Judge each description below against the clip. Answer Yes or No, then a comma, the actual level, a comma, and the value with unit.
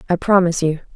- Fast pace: No, average, 190 wpm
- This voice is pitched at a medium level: Yes, medium, 175 Hz